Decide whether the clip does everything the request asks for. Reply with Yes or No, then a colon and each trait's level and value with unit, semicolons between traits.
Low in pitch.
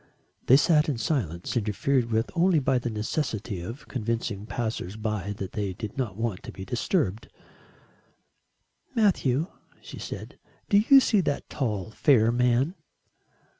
Yes: low, 115 Hz